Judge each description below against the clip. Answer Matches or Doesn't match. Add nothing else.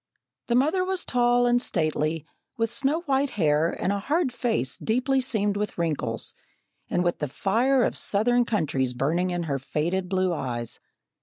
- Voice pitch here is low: Doesn't match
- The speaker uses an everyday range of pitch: Doesn't match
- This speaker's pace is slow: Doesn't match